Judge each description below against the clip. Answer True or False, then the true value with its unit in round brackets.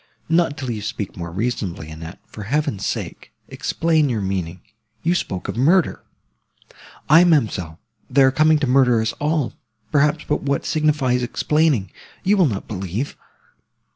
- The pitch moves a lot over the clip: True (7.5 semitones)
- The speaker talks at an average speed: True (145 wpm)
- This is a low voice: True (130 Hz)